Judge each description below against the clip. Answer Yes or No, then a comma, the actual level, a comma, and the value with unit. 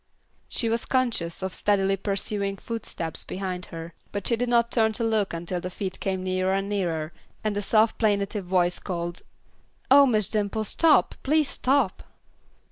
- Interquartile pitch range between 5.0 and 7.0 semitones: No, average, 3.5 semitones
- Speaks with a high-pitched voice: Yes, high, 200 Hz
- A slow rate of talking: No, average, 165 wpm